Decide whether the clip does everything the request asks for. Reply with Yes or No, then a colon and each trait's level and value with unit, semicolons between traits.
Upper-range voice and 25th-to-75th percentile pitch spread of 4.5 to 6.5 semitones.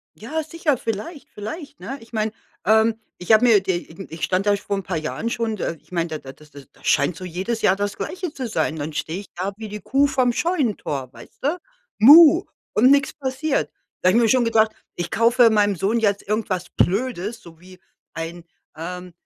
Yes: high, 215 Hz; wide, 5.6 semitones